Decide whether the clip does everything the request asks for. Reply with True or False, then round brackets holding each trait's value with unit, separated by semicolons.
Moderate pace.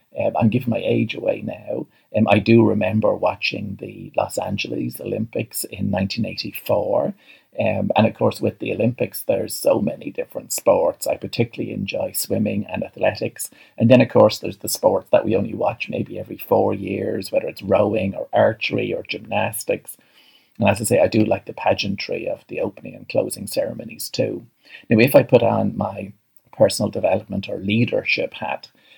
True (175 wpm)